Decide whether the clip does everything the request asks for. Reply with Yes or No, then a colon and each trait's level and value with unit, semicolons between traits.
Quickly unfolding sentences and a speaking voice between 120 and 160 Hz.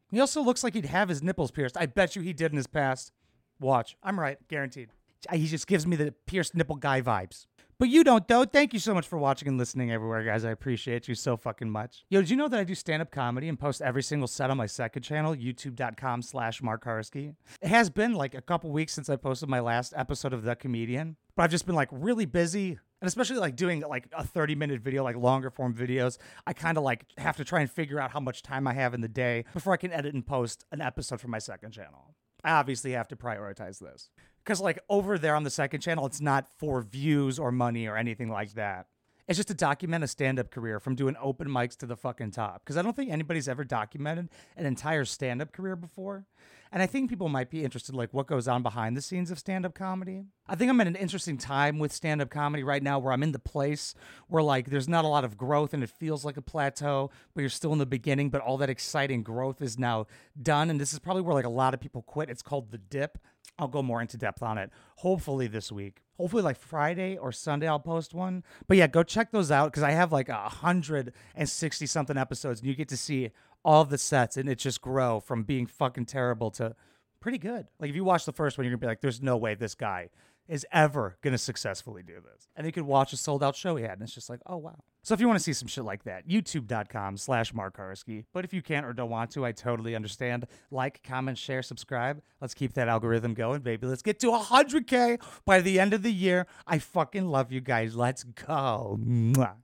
Yes: fast, 245 wpm; medium, 140 Hz